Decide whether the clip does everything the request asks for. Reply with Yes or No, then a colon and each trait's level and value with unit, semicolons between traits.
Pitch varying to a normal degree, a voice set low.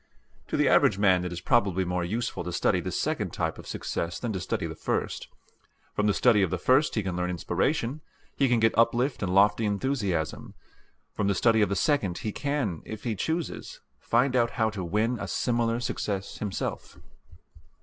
Yes: average, 4.3 semitones; low, 105 Hz